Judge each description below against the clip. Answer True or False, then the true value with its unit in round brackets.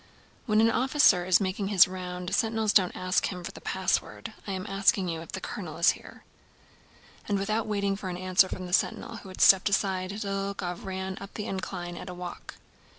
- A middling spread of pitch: False (1.8 semitones)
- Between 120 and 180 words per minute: False (205 wpm)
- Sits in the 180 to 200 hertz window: True (190 Hz)